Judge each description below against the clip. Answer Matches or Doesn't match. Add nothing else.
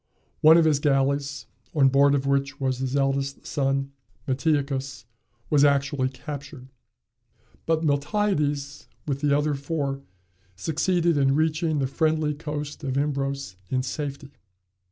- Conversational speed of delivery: Doesn't match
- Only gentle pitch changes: Matches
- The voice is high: Doesn't match